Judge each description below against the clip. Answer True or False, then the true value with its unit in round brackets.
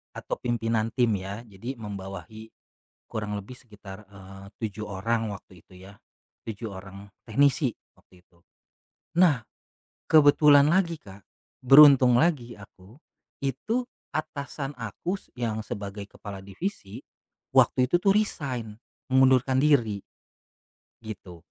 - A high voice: False (115 Hz)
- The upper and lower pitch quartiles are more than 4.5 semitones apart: True (5.5 semitones)